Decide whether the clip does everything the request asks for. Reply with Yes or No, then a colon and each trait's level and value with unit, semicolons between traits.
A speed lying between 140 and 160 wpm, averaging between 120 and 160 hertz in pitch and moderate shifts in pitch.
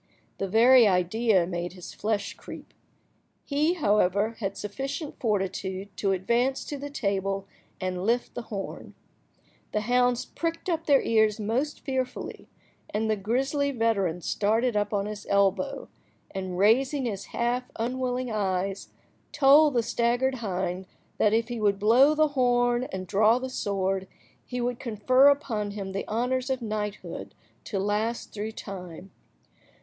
No: average, 145 wpm; high, 220 Hz; average, 4.3 semitones